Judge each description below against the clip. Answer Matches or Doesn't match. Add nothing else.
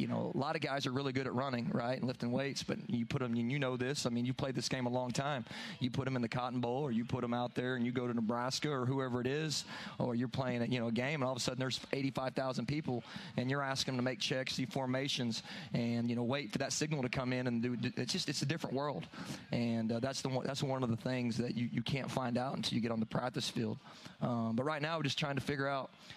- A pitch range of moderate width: Doesn't match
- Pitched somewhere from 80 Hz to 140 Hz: Matches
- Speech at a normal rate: Doesn't match